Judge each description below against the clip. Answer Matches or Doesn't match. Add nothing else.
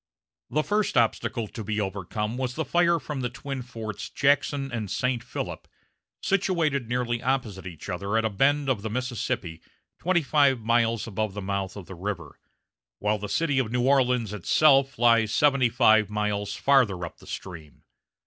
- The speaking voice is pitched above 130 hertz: Doesn't match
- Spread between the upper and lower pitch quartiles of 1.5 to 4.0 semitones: Doesn't match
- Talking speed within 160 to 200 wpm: Matches